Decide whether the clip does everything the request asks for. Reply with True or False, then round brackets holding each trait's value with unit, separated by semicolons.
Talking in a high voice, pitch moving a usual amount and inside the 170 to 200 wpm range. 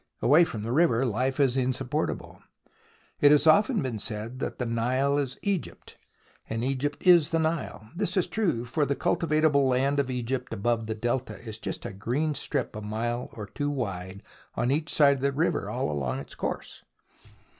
False (130 Hz; 4.2 semitones; 185 wpm)